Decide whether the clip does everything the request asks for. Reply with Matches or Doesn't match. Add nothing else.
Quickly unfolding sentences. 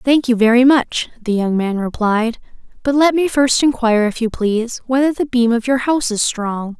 Matches